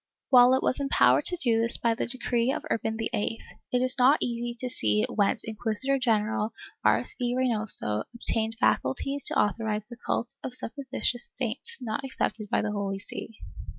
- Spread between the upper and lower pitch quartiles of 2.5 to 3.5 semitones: Yes, average, 2.8 semitones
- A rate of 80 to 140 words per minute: No, average, 175 wpm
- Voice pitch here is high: Yes, high, 235 Hz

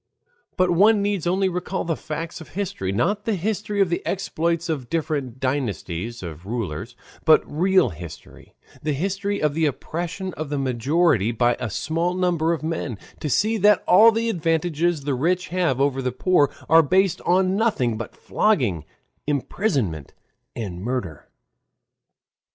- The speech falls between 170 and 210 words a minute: No, average, 155 wpm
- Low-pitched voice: No, medium, 160 Hz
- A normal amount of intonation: No, wide, 6.6 semitones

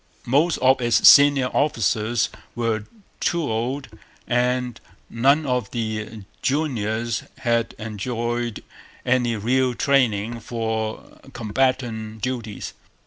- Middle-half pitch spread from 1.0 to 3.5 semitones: Yes, average, 2.7 semitones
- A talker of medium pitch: No, low, 120 Hz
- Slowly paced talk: Yes, slow, 95 wpm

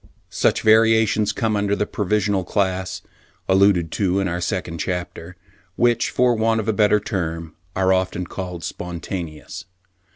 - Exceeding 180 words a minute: No, average, 140 wpm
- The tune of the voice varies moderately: Yes, average, 3.2 semitones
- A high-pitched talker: No, very low, 95 Hz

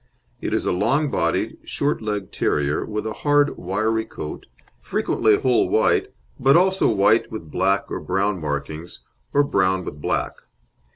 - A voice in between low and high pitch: No, low, 105 Hz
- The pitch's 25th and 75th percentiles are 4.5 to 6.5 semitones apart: Yes, wide, 5.5 semitones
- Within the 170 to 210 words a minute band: No, average, 155 wpm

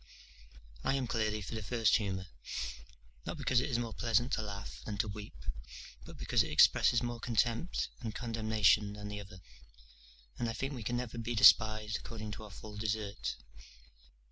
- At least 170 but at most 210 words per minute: Yes, average, 180 wpm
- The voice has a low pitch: Yes, low, 110 Hz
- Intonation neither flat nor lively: No, narrow, 2.3 semitones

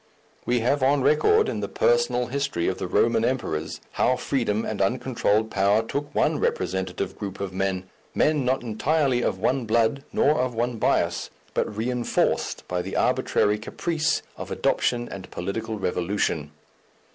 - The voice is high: No, low, 115 Hz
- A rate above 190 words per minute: No, average, 155 wpm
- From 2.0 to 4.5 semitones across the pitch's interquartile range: No, average, 5.0 semitones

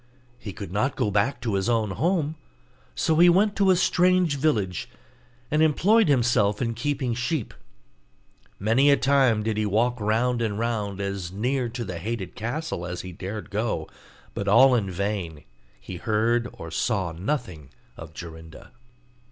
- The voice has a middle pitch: No, low, 115 Hz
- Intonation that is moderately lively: No, wide, 5.7 semitones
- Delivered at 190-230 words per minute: No, average, 160 wpm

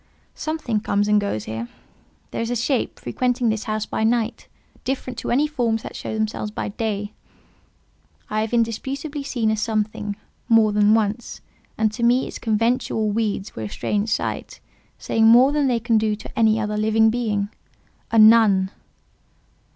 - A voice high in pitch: Yes, high, 220 Hz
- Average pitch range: No, narrow, 2.2 semitones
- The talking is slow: No, average, 165 wpm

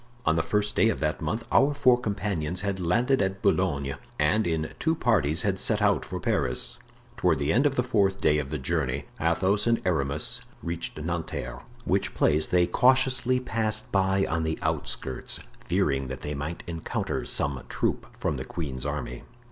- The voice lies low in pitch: Yes, very low, 85 Hz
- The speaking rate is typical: Yes, average, 180 wpm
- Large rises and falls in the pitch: Yes, wide, 6.2 semitones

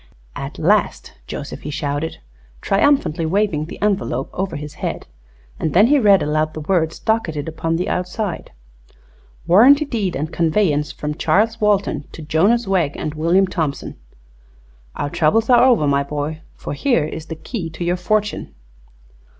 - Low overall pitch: No, medium, 165 Hz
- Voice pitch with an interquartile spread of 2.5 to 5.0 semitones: No, wide, 5.4 semitones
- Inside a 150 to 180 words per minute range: Yes, average, 155 wpm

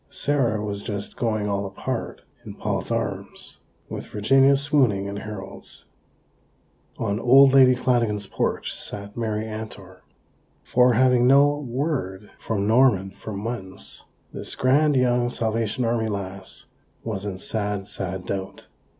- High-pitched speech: No, low, 110 Hz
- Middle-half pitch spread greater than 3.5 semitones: Yes, average, 4.0 semitones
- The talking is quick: No, slow, 135 wpm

